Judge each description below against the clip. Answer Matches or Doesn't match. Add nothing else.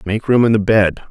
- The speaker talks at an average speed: Doesn't match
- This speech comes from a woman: Doesn't match